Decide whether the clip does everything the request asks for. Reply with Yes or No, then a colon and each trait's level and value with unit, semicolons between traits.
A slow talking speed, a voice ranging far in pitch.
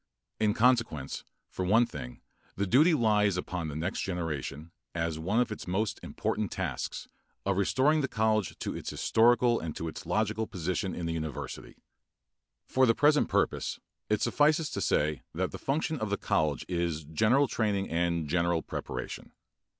No: average, 165 wpm; wide, 5.9 semitones